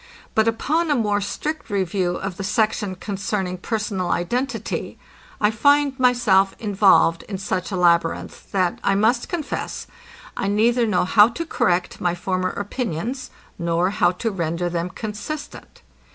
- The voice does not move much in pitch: No, average, 4.1 semitones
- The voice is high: Yes, high, 200 Hz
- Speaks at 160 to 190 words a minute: No, average, 145 wpm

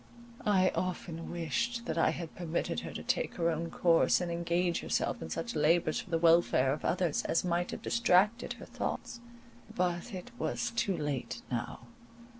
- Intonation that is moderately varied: No, narrow, 2.2 semitones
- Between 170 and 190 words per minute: Yes, average, 175 wpm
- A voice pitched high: No, medium, 170 Hz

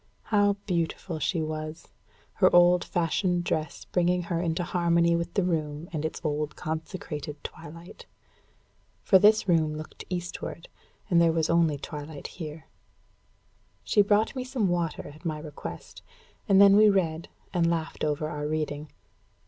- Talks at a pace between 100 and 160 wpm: Yes, average, 150 wpm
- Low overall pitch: No, medium, 165 Hz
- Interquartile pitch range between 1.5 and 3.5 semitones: Yes, narrow, 2.5 semitones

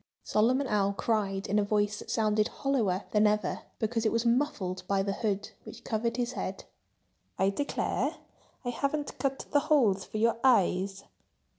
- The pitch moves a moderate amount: Yes, average, 3.6 semitones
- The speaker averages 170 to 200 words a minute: No, average, 160 wpm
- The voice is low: No, high, 215 Hz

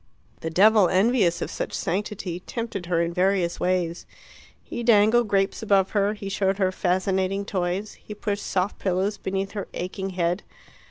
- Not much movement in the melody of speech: Yes, narrow, 2.2 semitones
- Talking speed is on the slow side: No, average, 160 wpm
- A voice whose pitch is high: Yes, high, 195 Hz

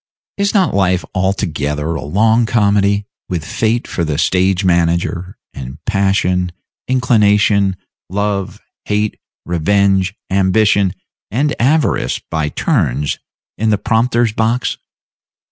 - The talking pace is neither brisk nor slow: No, slow, 110 wpm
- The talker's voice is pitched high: No, low, 100 Hz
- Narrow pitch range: No, average, 4.0 semitones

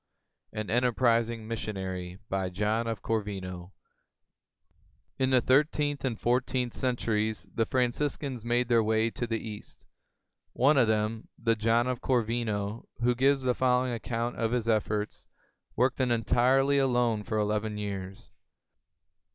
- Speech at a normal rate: No, slow, 120 wpm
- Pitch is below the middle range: Yes, low, 115 Hz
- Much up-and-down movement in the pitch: No, average, 2.7 semitones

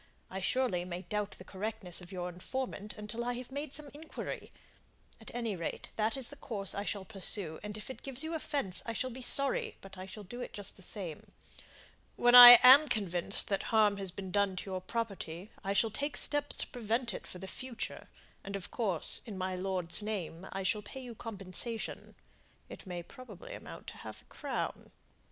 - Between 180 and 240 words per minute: Yes, average, 200 wpm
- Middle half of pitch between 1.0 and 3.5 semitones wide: No, average, 4.6 semitones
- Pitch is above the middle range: Yes, high, 210 Hz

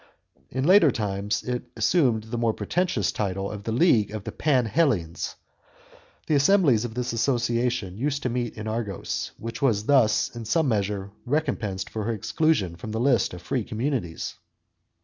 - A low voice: Yes, low, 115 Hz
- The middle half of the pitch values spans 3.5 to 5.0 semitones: Yes, average, 4.1 semitones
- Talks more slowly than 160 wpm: No, average, 165 wpm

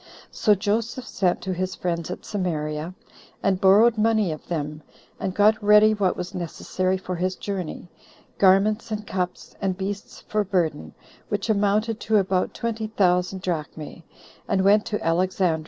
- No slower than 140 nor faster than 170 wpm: Yes, average, 155 wpm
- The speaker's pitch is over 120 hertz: Yes, high, 190 Hz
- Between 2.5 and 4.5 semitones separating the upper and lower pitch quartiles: Yes, average, 2.8 semitones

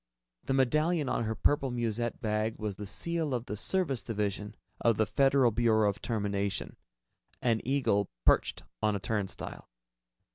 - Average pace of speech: Yes, average, 150 wpm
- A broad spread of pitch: No, average, 4.2 semitones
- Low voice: Yes, low, 115 Hz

